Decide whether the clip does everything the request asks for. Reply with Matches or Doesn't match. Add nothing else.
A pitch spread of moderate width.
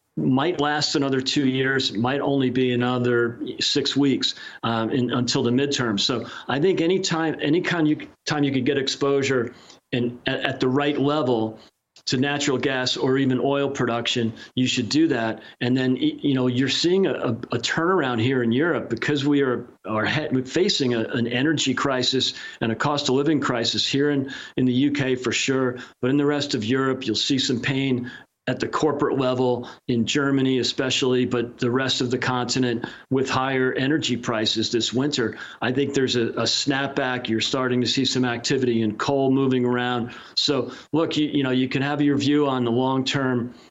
Doesn't match